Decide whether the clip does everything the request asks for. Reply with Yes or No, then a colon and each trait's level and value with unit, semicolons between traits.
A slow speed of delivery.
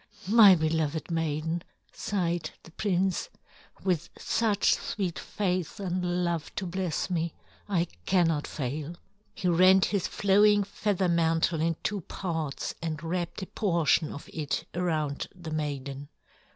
Yes: slow, 130 wpm